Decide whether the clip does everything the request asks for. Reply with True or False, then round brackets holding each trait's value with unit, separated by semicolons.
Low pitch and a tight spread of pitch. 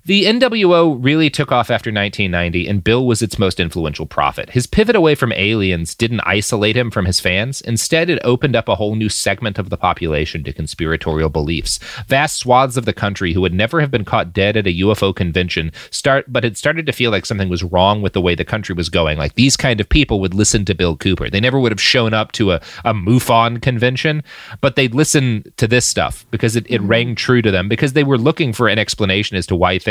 False (110 Hz; 5.3 semitones)